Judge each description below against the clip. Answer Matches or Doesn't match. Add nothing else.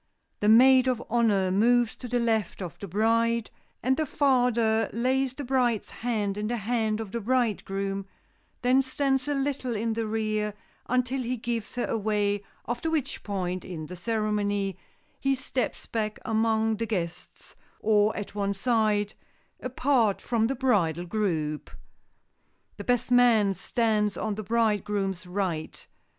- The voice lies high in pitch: Matches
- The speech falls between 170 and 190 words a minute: Doesn't match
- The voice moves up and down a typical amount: Matches